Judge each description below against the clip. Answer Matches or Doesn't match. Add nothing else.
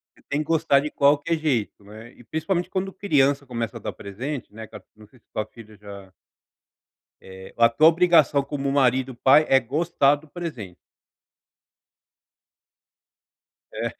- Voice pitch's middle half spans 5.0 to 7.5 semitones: Matches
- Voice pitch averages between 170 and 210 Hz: Doesn't match